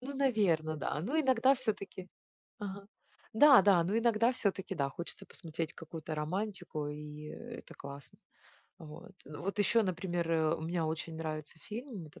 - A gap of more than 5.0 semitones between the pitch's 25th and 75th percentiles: Yes, wide, 5.6 semitones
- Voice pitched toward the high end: No, medium, 180 Hz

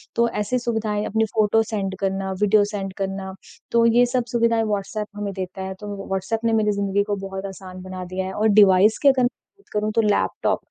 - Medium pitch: No, high, 205 Hz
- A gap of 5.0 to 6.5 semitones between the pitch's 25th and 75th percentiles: No, narrow, 2.5 semitones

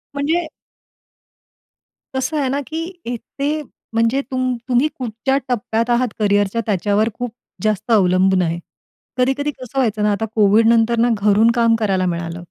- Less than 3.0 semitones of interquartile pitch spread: No, average, 3.9 semitones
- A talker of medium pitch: No, high, 230 Hz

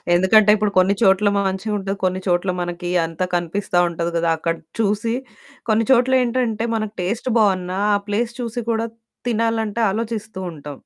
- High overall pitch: Yes, high, 205 Hz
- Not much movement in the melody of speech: No, average, 3.9 semitones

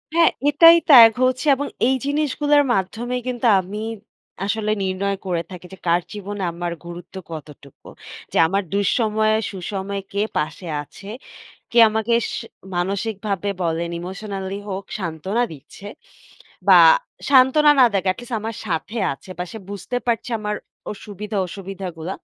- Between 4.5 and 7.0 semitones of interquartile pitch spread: No, average, 3.9 semitones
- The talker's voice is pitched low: No, high, 200 Hz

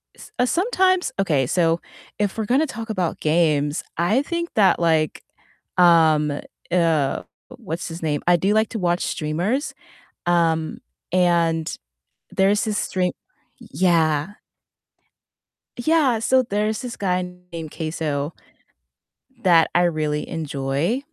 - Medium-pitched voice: Yes, medium, 175 Hz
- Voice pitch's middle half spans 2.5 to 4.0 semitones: No, average, 5.1 semitones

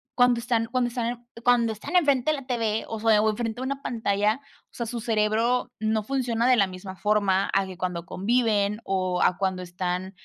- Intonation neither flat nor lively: Yes, average, 3.7 semitones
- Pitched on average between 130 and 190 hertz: No, high, 220 Hz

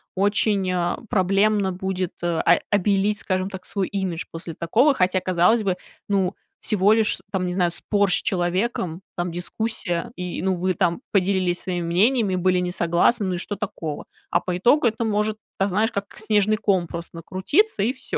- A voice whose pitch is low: No, high, 190 Hz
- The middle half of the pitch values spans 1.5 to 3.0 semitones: Yes, average, 2.7 semitones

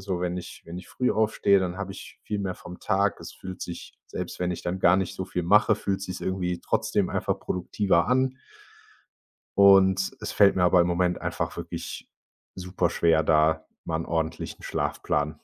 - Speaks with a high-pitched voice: No, very low, 90 Hz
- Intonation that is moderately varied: No, narrow, 1.9 semitones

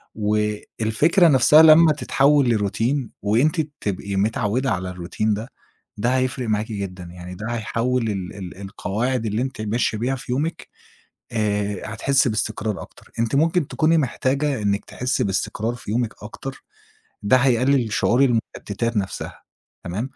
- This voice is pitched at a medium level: No, low, 115 Hz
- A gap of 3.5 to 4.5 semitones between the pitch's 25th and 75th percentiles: Yes, average, 4.2 semitones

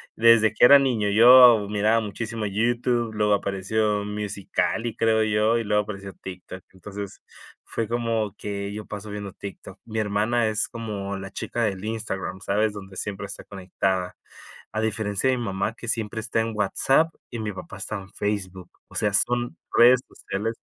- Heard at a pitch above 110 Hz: No, low, 105 Hz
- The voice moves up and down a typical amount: No, narrow, 2.3 semitones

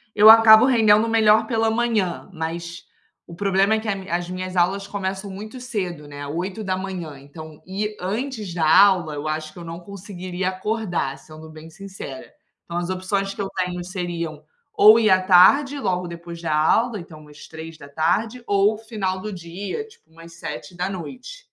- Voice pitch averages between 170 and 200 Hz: Yes, medium, 185 Hz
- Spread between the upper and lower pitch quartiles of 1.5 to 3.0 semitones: No, average, 4.0 semitones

